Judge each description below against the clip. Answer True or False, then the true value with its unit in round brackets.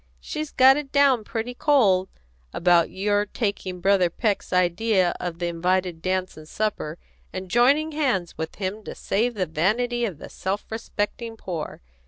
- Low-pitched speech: False (195 Hz)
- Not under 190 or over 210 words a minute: False (160 wpm)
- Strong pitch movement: False (4.9 semitones)